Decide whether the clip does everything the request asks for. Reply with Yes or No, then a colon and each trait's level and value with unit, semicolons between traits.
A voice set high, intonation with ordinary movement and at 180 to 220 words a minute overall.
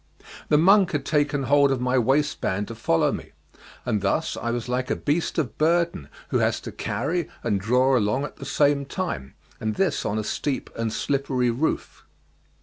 No: low, 135 Hz; average, 4.5 semitones; average, 185 wpm